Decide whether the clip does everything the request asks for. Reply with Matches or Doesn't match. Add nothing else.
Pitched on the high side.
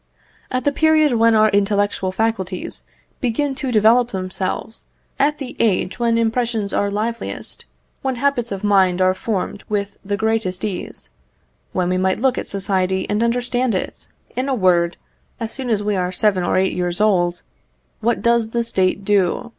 Matches